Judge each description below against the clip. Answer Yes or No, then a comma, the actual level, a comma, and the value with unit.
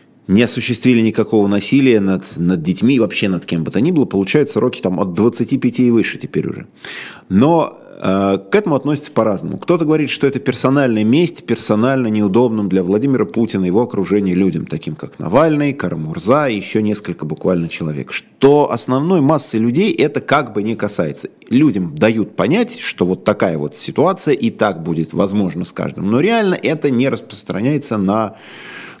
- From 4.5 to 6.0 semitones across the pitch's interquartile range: Yes, average, 5.0 semitones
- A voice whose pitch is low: Yes, low, 110 Hz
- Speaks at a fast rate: Yes, fast, 170 wpm